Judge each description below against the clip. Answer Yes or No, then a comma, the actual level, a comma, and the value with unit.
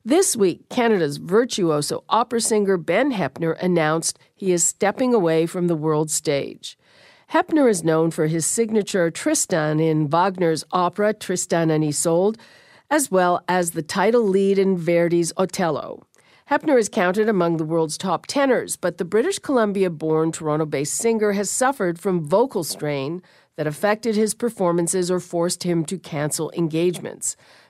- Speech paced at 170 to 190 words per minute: No, average, 145 wpm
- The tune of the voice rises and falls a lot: No, average, 4.7 semitones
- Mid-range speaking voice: Yes, medium, 180 Hz